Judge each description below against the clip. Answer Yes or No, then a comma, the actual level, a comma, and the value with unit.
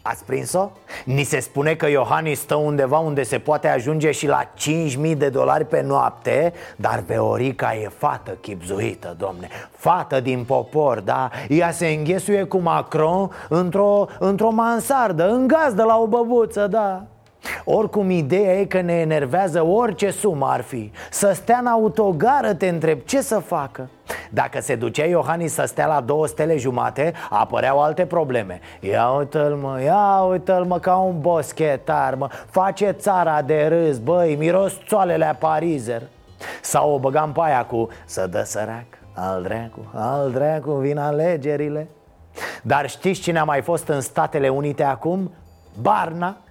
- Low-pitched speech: No, medium, 155 Hz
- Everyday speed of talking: Yes, average, 155 wpm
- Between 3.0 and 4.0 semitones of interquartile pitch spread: No, average, 5.2 semitones